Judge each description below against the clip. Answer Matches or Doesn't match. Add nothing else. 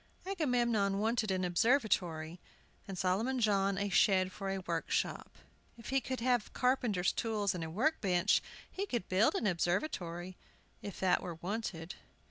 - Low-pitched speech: Doesn't match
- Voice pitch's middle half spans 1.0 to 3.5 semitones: Doesn't match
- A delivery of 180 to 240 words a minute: Doesn't match